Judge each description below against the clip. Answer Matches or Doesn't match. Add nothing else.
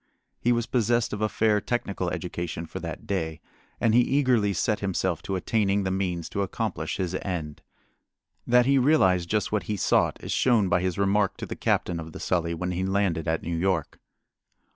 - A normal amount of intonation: Matches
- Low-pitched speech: Matches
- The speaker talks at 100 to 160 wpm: Doesn't match